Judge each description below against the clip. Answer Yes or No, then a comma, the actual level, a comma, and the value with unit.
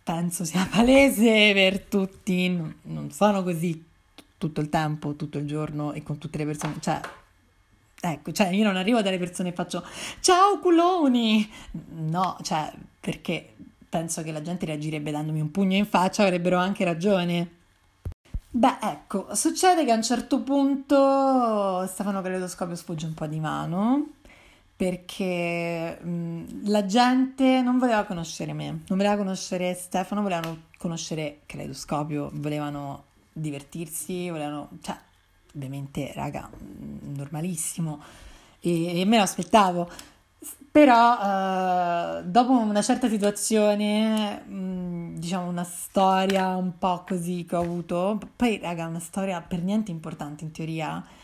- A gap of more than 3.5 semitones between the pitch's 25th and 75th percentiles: Yes, average, 4.5 semitones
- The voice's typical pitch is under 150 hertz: No, medium, 180 Hz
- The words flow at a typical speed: Yes, average, 135 wpm